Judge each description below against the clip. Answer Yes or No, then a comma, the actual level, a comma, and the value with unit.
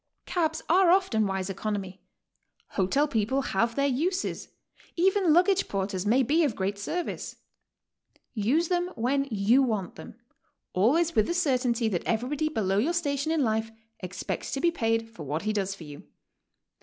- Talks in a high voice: Yes, high, 240 Hz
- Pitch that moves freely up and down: Yes, wide, 7.8 semitones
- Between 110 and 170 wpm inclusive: Yes, average, 165 wpm